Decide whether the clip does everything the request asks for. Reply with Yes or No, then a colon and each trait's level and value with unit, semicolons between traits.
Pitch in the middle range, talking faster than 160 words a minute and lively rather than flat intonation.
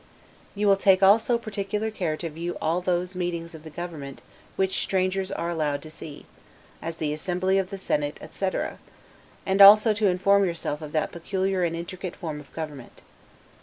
No: medium, 180 Hz; average, 175 wpm; average, 3.3 semitones